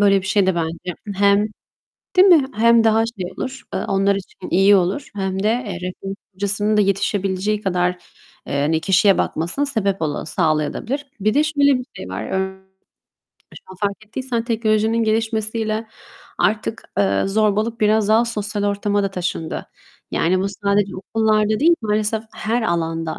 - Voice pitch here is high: Yes, high, 205 Hz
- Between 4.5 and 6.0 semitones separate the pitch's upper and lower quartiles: No, average, 2.7 semitones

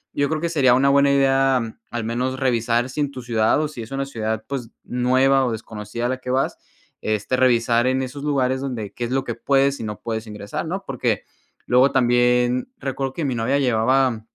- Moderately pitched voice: No, low, 125 Hz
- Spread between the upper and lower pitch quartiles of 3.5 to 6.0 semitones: No, narrow, 2.6 semitones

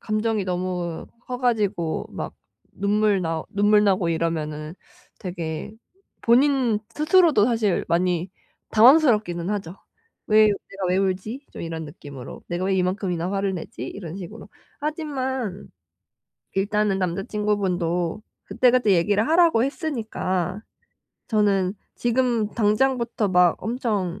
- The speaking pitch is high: Yes, high, 200 Hz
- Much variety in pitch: No, average, 4.2 semitones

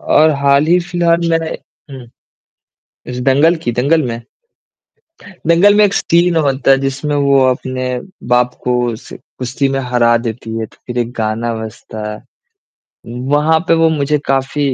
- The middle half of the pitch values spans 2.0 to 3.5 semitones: No, average, 4.6 semitones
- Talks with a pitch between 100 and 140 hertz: Yes, low, 135 Hz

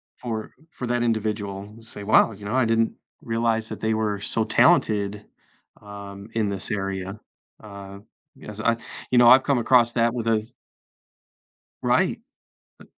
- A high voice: No, low, 110 Hz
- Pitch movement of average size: No, narrow, 2.3 semitones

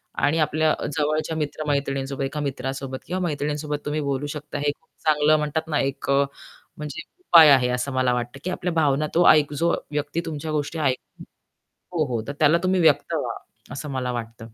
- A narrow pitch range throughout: Yes, narrow, 2.2 semitones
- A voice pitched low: No, medium, 145 Hz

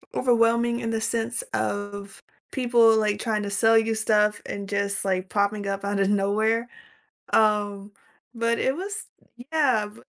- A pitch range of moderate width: No, narrow, 2.3 semitones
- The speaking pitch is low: No, high, 215 Hz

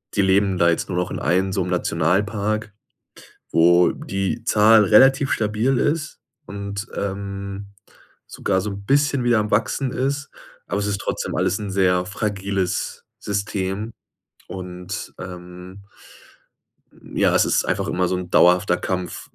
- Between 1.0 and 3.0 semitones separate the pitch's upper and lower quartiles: Yes, narrow, 2.6 semitones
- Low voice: Yes, low, 100 Hz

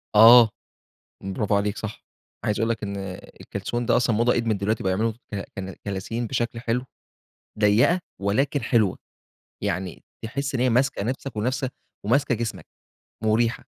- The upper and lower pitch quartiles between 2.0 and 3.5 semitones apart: Yes, average, 2.9 semitones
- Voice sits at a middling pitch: No, low, 115 Hz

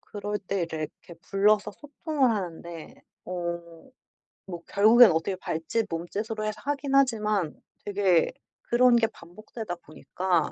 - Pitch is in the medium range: No, high, 205 Hz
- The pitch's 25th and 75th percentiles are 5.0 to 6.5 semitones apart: No, average, 4.5 semitones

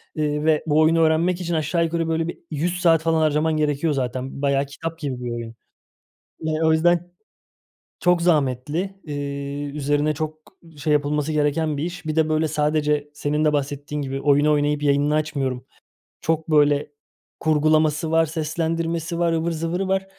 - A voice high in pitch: No, medium, 155 Hz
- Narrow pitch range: Yes, narrow, 2.0 semitones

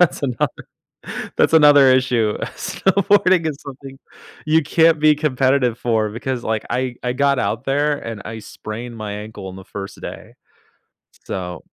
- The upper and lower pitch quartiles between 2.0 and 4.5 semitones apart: No, average, 4.9 semitones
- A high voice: No, low, 130 Hz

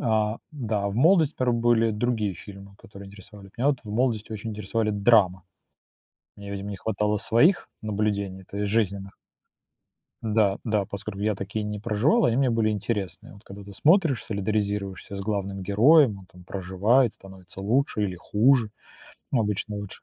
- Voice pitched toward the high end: No, low, 105 Hz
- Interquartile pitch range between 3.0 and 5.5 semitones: No, narrow, 2.4 semitones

